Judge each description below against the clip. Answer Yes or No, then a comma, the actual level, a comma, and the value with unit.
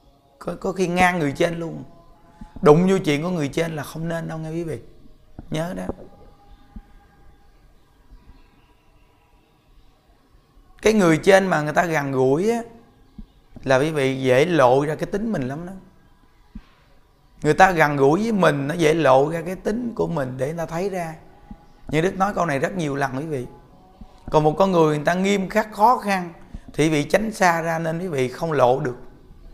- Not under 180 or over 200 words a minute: Yes, average, 185 wpm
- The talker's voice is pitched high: No, medium, 160 Hz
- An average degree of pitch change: Yes, average, 4.9 semitones